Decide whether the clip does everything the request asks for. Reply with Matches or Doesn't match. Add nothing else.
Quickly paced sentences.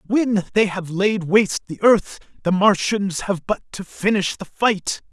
Doesn't match